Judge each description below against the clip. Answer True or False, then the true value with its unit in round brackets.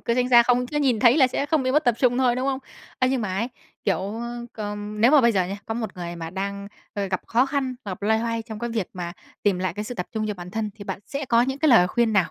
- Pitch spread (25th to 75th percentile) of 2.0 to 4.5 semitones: True (4.1 semitones)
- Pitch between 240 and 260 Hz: False (230 Hz)